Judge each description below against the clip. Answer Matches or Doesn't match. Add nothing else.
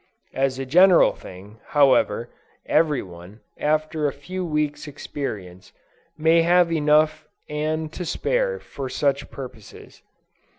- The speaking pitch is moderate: Matches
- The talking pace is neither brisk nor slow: Doesn't match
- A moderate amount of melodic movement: Matches